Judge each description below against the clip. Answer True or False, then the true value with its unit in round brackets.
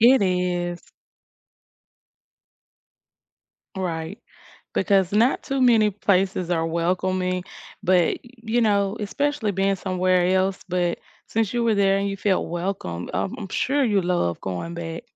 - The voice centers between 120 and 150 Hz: False (190 Hz)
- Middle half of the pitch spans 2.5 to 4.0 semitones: True (2.9 semitones)